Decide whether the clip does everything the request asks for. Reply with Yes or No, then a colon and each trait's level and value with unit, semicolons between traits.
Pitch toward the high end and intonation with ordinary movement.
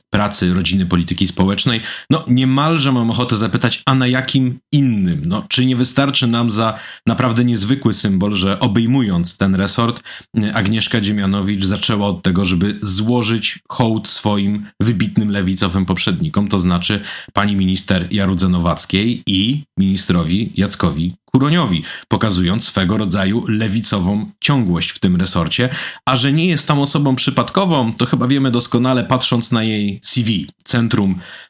No: low, 110 Hz; average, 4.8 semitones